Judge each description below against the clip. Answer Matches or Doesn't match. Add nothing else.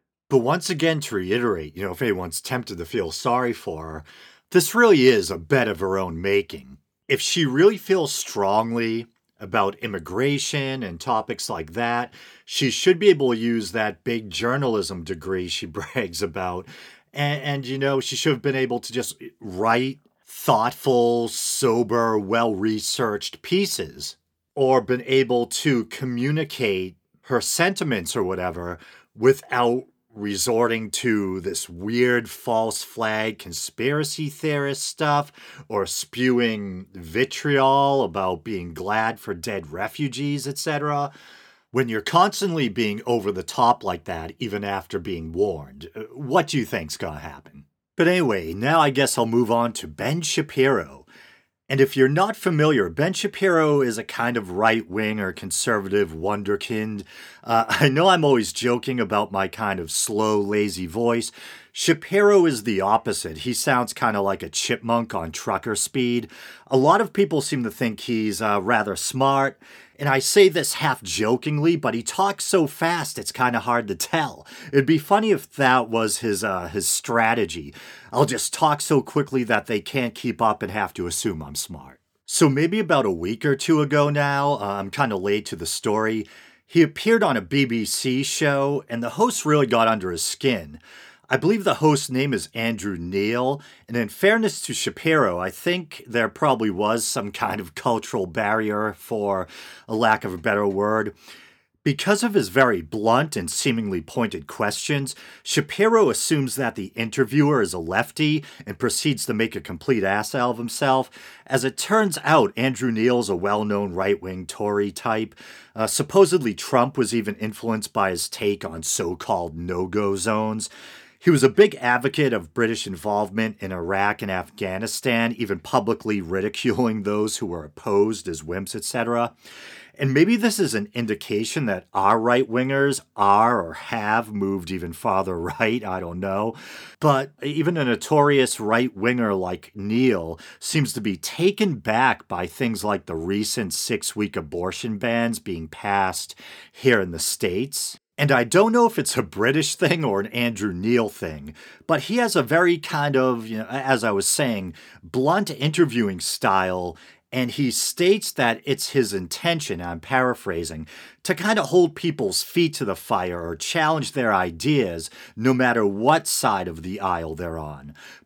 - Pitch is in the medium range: Doesn't match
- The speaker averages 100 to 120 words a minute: Doesn't match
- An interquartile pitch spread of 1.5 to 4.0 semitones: Doesn't match